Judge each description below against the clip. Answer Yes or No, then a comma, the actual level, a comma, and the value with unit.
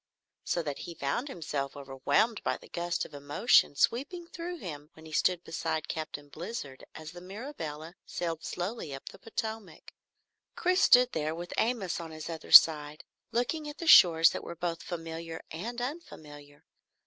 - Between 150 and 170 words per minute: Yes, average, 165 wpm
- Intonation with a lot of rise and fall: Yes, wide, 6.8 semitones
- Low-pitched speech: No, medium, 170 Hz